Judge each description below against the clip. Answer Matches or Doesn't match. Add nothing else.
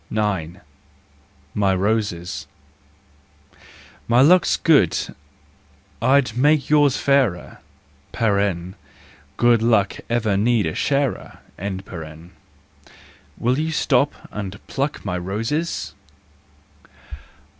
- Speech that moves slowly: Matches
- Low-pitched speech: Matches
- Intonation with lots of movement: Matches